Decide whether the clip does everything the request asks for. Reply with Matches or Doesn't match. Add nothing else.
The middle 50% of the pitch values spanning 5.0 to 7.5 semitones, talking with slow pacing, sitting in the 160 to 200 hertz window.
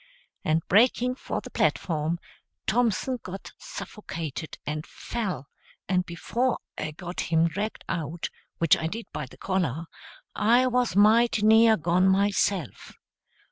Matches